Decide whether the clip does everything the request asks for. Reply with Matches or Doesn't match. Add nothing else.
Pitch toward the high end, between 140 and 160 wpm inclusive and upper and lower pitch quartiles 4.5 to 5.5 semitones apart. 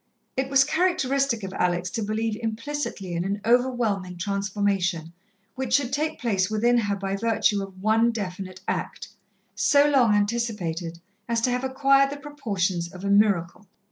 Matches